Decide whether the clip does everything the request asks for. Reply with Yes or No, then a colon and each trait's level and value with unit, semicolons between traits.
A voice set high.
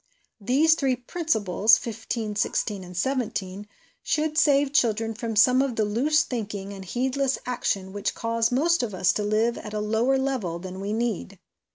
Yes: high, 225 Hz